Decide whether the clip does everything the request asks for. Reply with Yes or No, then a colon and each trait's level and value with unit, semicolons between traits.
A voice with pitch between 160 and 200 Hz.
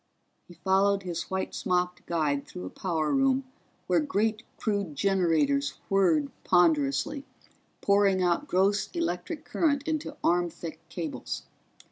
Yes: medium, 185 Hz